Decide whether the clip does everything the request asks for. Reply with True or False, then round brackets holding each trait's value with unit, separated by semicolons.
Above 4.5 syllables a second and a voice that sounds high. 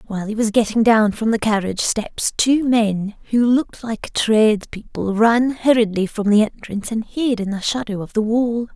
True (4.9 syllables/s; 220 Hz)